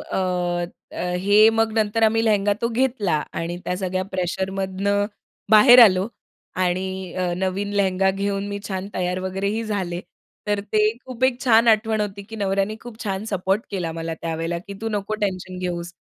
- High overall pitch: Yes, high, 195 Hz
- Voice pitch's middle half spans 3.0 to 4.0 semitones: No, narrow, 2.6 semitones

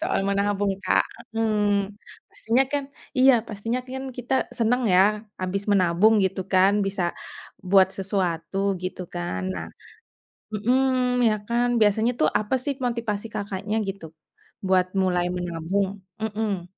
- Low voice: No, high, 205 Hz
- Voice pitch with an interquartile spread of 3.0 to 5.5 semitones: Yes, average, 3.7 semitones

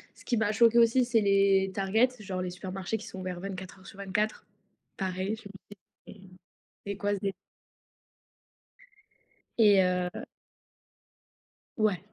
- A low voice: No, high, 195 Hz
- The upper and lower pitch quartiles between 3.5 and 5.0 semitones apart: No, narrow, 2.5 semitones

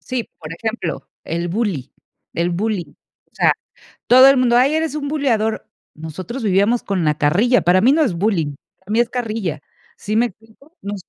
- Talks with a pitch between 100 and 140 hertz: No, high, 215 Hz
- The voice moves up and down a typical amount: No, wide, 5.9 semitones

